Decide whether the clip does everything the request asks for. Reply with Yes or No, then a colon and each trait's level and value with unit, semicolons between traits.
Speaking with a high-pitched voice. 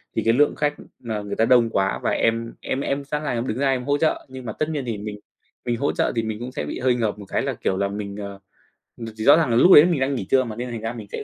No: low, 120 Hz